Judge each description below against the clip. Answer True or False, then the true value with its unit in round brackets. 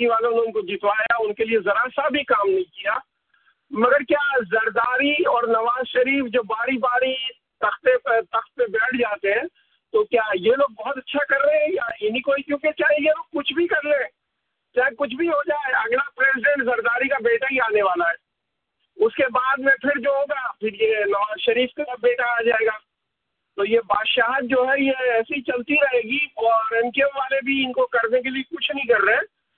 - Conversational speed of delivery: False (215 wpm)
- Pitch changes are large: False (4.0 semitones)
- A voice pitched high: True (265 Hz)